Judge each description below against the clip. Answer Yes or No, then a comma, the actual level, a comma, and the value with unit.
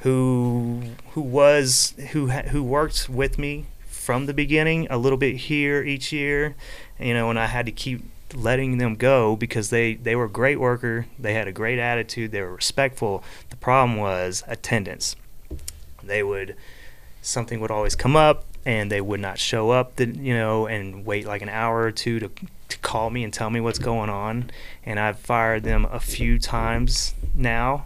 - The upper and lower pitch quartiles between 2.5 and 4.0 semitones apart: Yes, average, 3.0 semitones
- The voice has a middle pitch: No, low, 120 Hz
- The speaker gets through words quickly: No, average, 190 wpm